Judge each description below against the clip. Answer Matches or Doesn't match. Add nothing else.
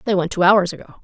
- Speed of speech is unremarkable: Doesn't match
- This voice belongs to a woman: Matches